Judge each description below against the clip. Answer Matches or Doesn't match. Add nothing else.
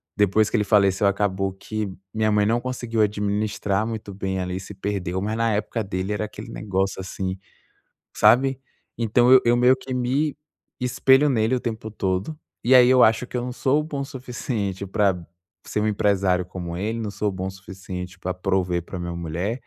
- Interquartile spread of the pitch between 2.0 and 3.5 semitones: Doesn't match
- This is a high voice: Doesn't match